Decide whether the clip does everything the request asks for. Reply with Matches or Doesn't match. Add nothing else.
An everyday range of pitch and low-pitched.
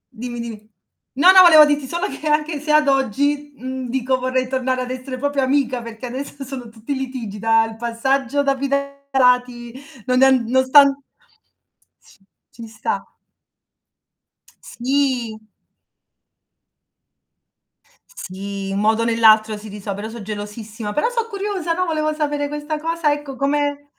Doesn't match